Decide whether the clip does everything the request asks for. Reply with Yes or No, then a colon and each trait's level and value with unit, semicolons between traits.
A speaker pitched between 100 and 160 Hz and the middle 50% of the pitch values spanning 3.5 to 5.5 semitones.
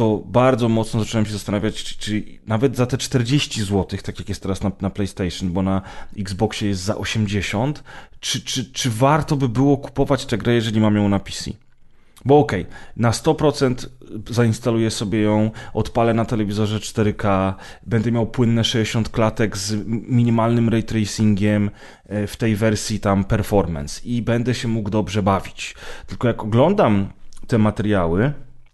No: low, 110 Hz; average, 2.7 semitones